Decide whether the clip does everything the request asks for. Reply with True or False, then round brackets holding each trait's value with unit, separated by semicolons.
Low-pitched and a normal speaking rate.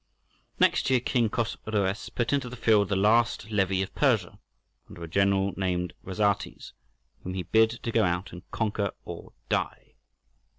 True (100 Hz; 160 wpm)